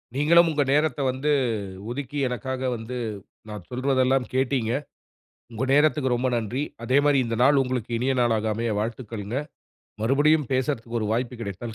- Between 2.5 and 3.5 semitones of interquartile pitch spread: Yes, average, 3.2 semitones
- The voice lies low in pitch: Yes, low, 130 Hz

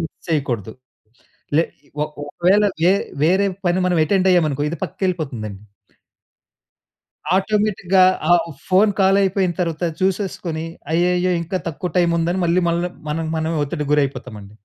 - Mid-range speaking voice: Yes, medium, 170 Hz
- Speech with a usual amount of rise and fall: Yes, average, 3.3 semitones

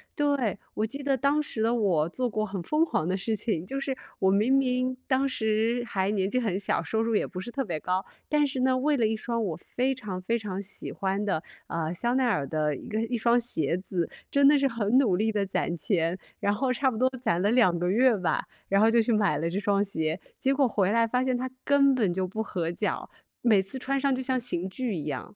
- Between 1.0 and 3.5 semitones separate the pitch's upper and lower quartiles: No, average, 5.3 semitones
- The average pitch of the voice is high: Yes, high, 220 Hz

